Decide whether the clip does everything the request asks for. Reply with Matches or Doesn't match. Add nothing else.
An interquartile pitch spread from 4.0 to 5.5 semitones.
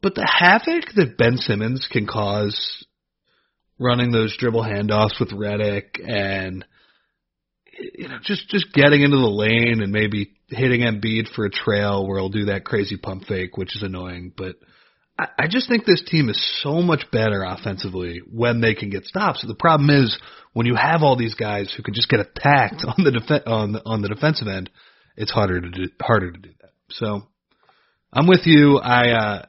Matches